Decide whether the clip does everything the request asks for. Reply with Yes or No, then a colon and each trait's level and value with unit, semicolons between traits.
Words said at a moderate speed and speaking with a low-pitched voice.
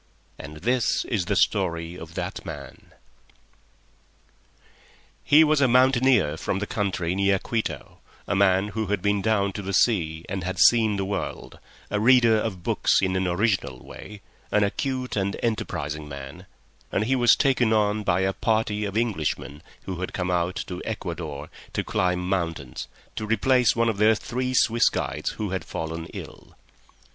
Yes: average, 165 wpm; low, 100 Hz